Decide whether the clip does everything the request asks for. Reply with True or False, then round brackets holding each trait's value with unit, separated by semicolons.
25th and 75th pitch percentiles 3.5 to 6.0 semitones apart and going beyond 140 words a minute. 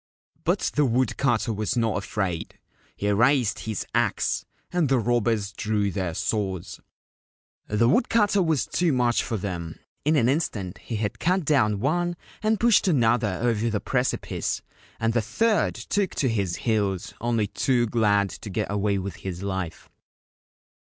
True (4.9 semitones; 155 wpm)